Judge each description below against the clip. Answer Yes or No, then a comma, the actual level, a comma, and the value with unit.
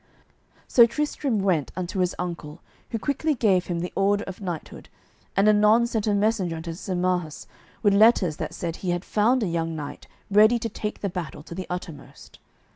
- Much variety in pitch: No, average, 3.8 semitones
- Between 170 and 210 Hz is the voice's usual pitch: Yes, high, 190 Hz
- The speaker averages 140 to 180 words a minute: No, average, 190 wpm